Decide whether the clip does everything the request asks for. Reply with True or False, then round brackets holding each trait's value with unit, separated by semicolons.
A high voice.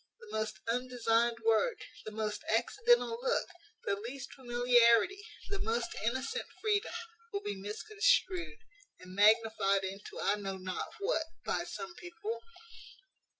True (235 Hz)